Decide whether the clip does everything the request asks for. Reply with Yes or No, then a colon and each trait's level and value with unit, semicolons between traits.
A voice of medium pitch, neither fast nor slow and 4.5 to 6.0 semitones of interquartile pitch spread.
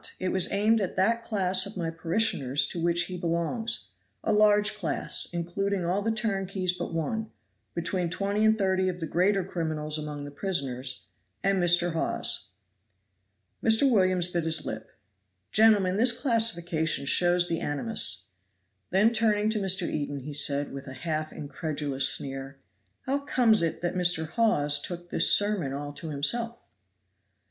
Yes: medium, 180 Hz; average, 155 wpm; average, 5.1 semitones